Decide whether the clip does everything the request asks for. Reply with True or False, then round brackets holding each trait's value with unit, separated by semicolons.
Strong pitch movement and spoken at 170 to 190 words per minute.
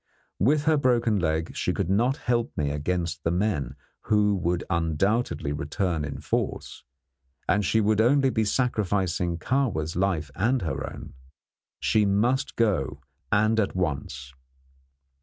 False (5.9 semitones; 140 wpm)